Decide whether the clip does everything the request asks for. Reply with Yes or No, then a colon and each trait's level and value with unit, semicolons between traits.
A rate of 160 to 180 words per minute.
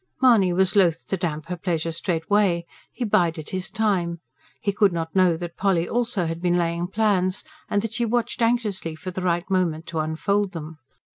No: average, 190 wpm